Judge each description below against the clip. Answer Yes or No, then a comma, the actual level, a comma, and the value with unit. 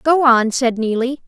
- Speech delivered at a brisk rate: No, average, 190 wpm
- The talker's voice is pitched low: No, very high, 250 Hz